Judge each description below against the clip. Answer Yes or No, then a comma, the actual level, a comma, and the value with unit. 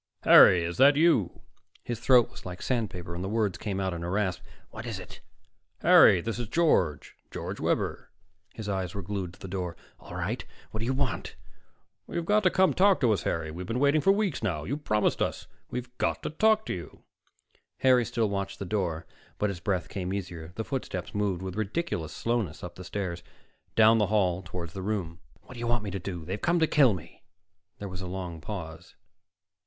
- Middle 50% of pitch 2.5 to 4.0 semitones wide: No, average, 5.1 semitones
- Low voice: Yes, low, 100 Hz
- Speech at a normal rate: No, fast, 210 wpm